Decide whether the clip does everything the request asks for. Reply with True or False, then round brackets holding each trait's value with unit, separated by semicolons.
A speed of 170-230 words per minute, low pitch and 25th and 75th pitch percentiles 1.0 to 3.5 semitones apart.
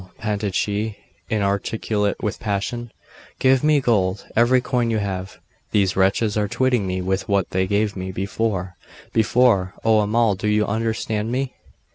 False (145 wpm; 105 Hz; 2.6 semitones)